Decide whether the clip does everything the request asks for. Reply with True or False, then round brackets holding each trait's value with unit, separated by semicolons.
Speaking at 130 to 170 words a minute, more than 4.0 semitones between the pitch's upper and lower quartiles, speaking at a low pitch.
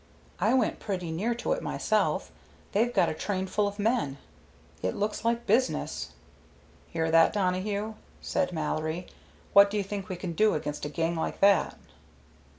False (165 wpm; 4.5 semitones; 200 Hz)